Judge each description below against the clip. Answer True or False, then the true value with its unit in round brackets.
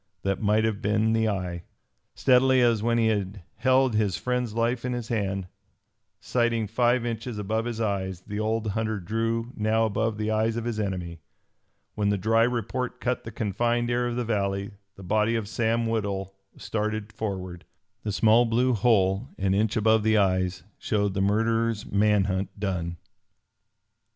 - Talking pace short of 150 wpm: False (170 wpm)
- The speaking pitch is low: True (110 Hz)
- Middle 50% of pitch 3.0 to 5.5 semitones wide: False (2.5 semitones)